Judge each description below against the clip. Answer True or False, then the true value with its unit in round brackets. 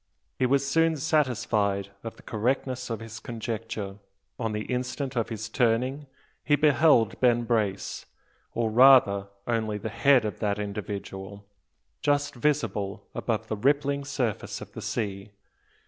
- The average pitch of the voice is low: True (115 Hz)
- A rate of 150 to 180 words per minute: False (140 wpm)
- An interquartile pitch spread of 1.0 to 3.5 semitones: False (4.3 semitones)